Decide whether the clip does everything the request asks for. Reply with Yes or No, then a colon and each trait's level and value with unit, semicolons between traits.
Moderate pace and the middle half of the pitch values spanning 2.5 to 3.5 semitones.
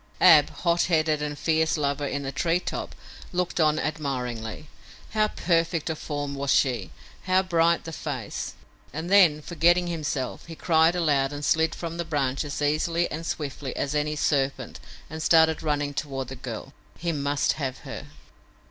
Yes: average, 165 wpm; average, 2.8 semitones